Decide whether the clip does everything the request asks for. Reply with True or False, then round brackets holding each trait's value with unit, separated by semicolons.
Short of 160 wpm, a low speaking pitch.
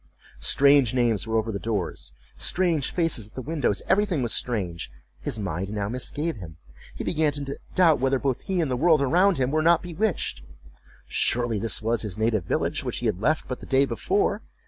False (190 wpm; 130 Hz)